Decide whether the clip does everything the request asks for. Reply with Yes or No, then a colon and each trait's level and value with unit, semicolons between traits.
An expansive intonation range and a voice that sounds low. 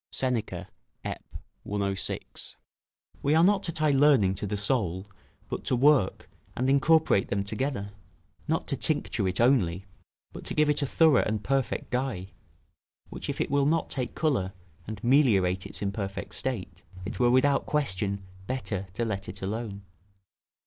Yes: wide, 6.0 semitones; low, 120 Hz